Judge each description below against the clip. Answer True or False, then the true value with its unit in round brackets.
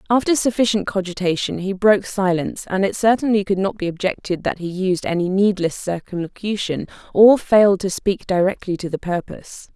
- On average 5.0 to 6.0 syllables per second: True (5.5 syllables/s)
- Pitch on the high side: True (195 Hz)